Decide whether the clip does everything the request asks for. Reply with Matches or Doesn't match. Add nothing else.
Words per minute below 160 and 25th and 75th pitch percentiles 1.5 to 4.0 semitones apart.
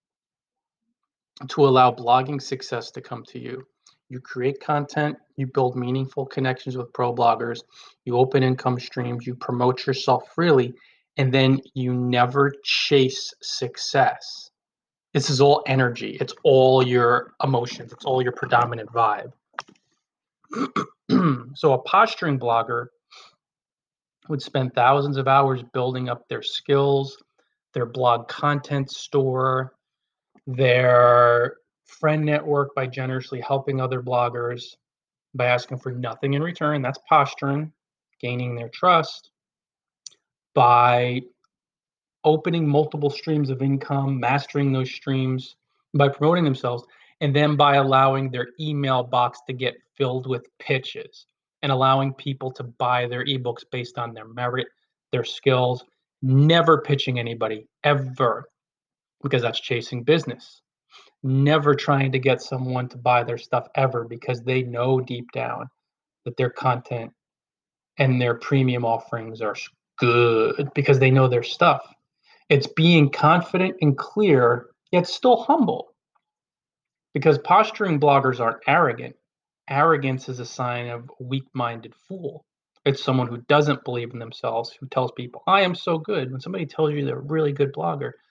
Matches